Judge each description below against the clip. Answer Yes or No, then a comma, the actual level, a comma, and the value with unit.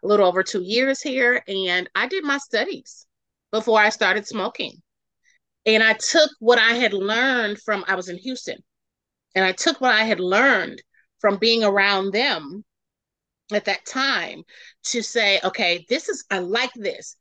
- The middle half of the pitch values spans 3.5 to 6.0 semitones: Yes, average, 4.4 semitones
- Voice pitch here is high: Yes, high, 220 Hz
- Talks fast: No, average, 170 wpm